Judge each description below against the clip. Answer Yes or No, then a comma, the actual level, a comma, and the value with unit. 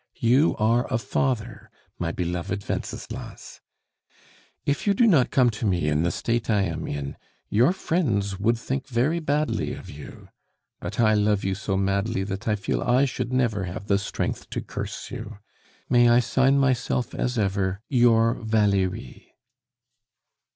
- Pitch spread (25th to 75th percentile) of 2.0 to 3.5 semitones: No, average, 4.2 semitones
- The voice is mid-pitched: No, low, 110 Hz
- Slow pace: No, average, 160 wpm